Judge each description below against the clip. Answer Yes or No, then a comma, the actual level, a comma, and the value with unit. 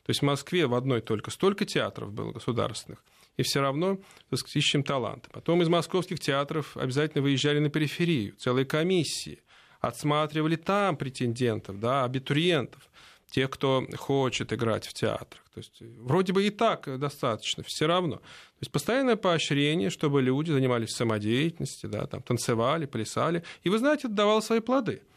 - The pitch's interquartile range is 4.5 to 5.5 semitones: Yes, average, 5.1 semitones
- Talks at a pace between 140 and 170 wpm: Yes, average, 155 wpm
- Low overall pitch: No, medium, 145 Hz